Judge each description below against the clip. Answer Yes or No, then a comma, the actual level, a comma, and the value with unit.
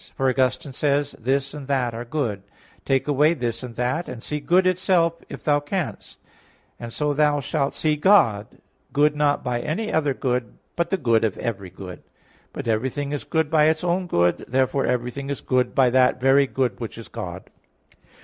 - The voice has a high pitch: No, low, 135 Hz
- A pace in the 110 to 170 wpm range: No, average, 195 wpm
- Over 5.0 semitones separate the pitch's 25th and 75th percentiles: No, average, 3.7 semitones